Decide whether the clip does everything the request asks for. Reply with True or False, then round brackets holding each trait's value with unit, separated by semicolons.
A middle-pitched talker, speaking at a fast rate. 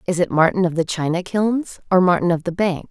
True (180 Hz; 250 wpm)